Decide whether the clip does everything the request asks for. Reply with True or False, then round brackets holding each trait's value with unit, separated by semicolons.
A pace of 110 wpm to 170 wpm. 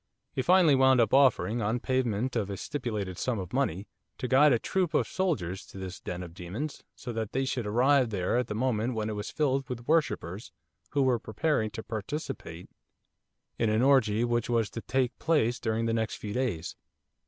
False (200 wpm)